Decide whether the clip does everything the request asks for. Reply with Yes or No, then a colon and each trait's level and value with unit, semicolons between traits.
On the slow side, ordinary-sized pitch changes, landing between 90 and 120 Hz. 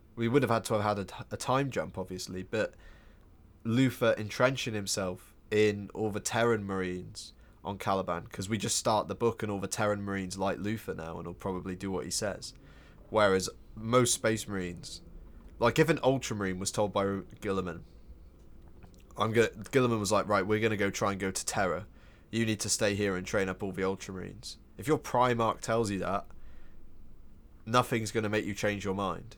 No: average, 200 wpm; average, 3.2 semitones; low, 100 Hz